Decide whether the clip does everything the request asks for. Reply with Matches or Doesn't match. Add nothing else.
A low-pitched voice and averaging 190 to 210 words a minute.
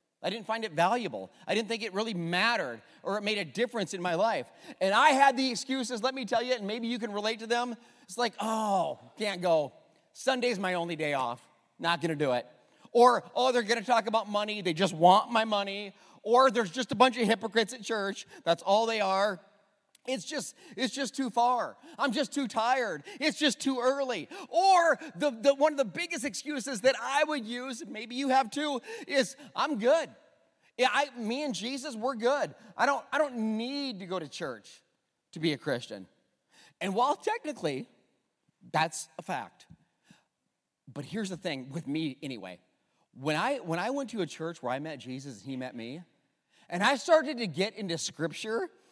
Doesn't match